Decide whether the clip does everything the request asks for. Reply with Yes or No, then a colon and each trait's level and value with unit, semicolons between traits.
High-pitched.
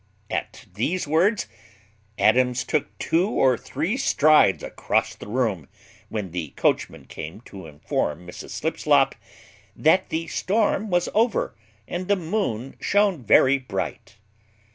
No: medium, 145 Hz